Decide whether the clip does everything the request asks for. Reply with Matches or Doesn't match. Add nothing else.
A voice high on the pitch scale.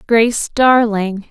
Matches